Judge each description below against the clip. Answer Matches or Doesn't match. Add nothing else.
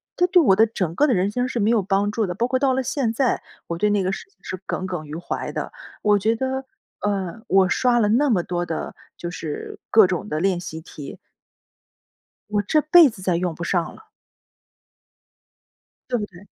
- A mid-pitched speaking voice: Doesn't match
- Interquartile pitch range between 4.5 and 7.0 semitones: Matches